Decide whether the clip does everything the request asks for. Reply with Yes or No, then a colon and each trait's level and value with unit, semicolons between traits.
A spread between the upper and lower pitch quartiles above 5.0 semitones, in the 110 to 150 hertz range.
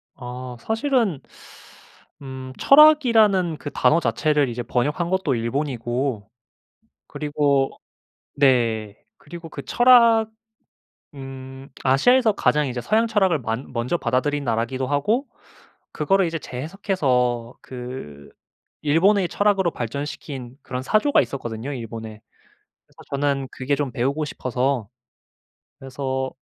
Yes: wide, 5.6 semitones; medium, 140 Hz